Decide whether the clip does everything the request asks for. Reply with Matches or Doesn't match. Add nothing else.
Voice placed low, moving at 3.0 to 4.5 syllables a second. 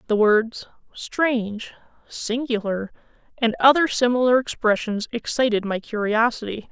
Doesn't match